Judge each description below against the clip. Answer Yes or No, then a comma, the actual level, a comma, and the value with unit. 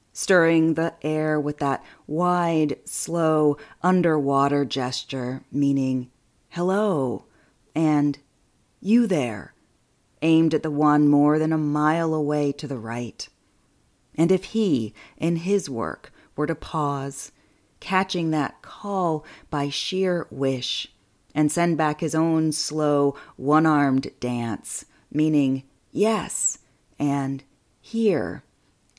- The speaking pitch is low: No, medium, 150 Hz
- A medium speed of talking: No, slow, 110 wpm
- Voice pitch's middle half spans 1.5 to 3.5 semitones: Yes, average, 3.1 semitones